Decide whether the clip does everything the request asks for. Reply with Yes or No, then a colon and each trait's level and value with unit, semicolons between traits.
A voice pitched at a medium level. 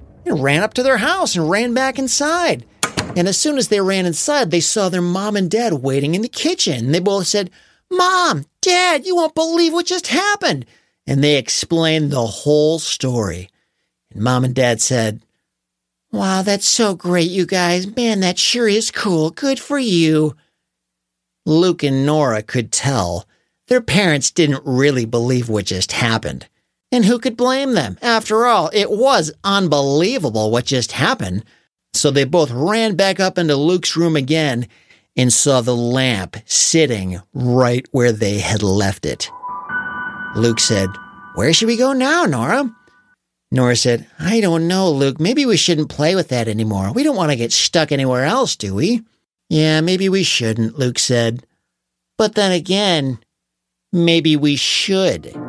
Yes: medium, 160 Hz